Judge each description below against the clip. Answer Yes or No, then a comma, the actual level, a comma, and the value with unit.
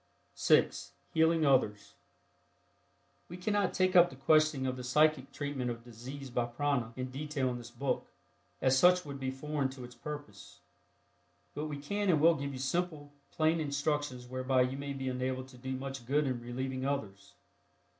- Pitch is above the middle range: No, low, 135 Hz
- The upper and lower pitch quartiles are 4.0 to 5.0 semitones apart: No, average, 2.8 semitones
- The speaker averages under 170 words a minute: No, average, 175 wpm